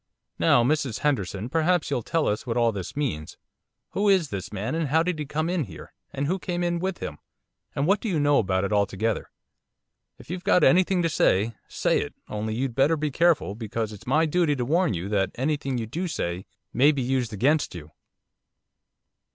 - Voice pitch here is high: No, medium, 140 Hz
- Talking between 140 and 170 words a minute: No, fast, 205 wpm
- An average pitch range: No, wide, 7.2 semitones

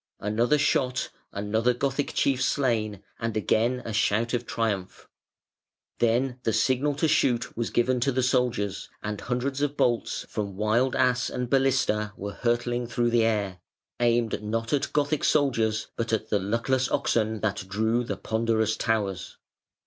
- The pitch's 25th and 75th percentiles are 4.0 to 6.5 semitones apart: No, average, 2.8 semitones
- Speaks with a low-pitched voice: Yes, low, 115 Hz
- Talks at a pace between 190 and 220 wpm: No, average, 155 wpm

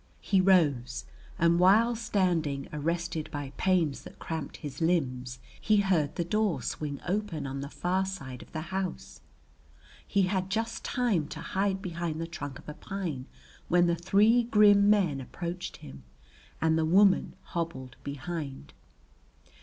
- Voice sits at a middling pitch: Yes, medium, 170 Hz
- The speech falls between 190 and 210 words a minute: No, average, 150 wpm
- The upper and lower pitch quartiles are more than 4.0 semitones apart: Yes, average, 4.7 semitones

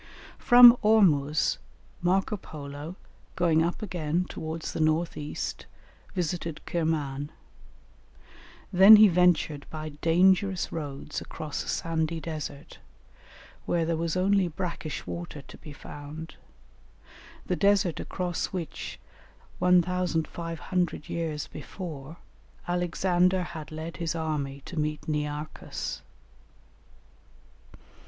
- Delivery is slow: Yes, slow, 100 wpm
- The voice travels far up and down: No, average, 2.8 semitones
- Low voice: No, medium, 165 Hz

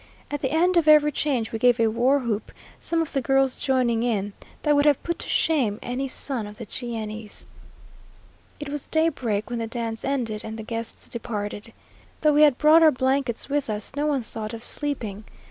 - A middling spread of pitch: Yes, average, 4.5 semitones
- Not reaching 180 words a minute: No, average, 200 wpm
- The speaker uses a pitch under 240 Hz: No, very high, 250 Hz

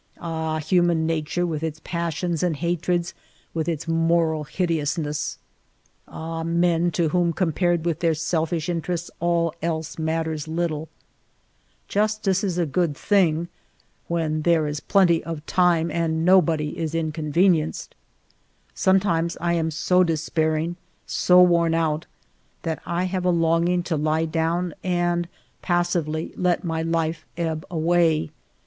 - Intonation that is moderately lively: No, narrow, 1.6 semitones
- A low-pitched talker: No, medium, 165 Hz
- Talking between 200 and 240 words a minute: No, slow, 135 wpm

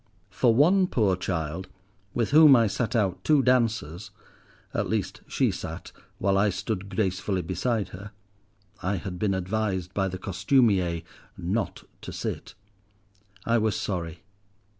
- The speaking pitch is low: Yes, low, 100 Hz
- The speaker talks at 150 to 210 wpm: No, slow, 135 wpm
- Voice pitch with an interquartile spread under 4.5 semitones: Yes, average, 3.5 semitones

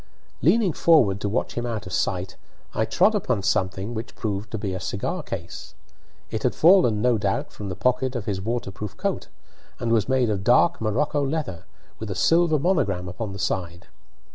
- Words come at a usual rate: Yes, average, 190 wpm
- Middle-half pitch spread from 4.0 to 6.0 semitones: Yes, average, 5.2 semitones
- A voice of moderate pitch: No, low, 110 Hz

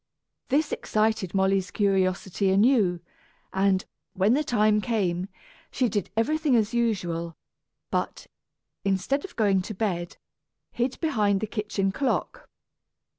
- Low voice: No, high, 205 Hz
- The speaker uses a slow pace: Yes, slow, 125 wpm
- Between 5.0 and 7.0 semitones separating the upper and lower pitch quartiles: No, average, 3.7 semitones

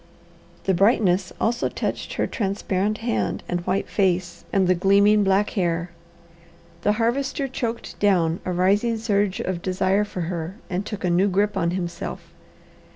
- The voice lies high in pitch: Yes, high, 195 Hz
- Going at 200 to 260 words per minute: No, average, 155 wpm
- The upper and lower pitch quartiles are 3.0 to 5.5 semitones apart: No, narrow, 2.5 semitones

